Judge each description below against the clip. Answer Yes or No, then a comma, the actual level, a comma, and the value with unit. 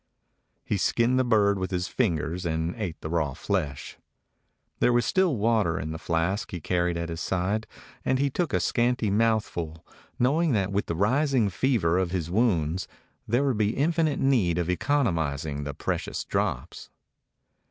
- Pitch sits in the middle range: No, low, 100 Hz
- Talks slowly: No, average, 170 wpm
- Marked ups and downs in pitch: Yes, wide, 6.3 semitones